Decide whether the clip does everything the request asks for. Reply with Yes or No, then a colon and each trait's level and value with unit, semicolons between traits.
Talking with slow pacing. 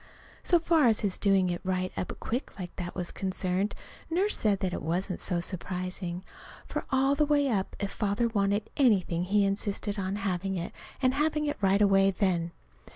No: average, 180 wpm